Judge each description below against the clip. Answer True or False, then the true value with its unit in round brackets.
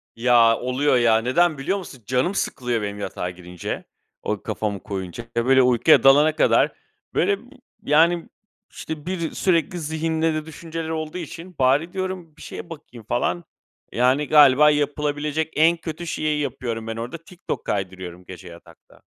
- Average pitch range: False (5.7 semitones)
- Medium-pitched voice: True (145 Hz)